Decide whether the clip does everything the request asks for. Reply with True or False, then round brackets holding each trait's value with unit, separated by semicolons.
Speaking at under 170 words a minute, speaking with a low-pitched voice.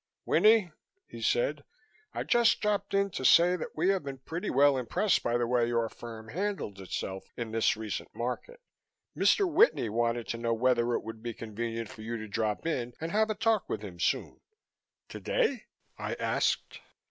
False (180 wpm; 120 Hz)